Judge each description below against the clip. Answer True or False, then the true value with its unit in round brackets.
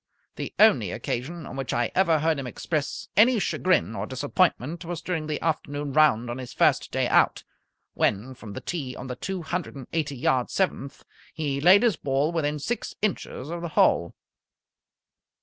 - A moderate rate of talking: True (180 wpm)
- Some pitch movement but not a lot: True (4.6 semitones)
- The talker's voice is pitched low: False (150 Hz)